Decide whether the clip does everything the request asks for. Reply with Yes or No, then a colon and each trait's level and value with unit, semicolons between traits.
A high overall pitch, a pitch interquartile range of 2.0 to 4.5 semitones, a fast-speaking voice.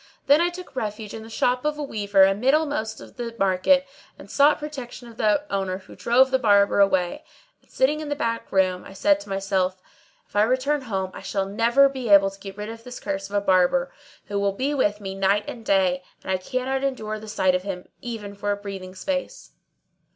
No: high, 210 Hz; average, 5.0 semitones; fast, 220 wpm